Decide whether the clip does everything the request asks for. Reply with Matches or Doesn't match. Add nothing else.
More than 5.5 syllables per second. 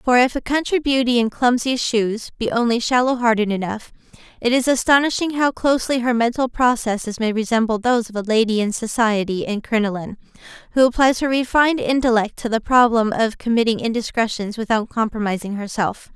Matches